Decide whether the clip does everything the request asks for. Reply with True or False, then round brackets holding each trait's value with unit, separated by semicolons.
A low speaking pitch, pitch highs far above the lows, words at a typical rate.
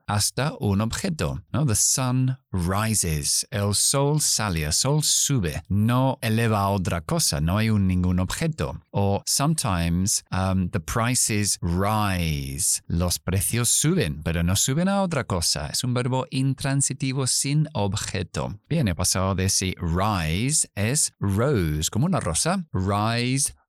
True (105 Hz; 6.3 semitones; 140 wpm)